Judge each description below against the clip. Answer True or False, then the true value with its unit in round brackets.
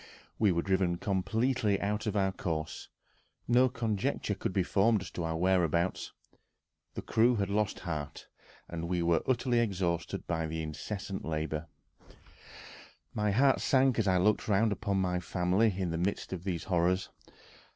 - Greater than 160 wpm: False (150 wpm)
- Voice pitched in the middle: False (95 Hz)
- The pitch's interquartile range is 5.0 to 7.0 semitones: False (3.8 semitones)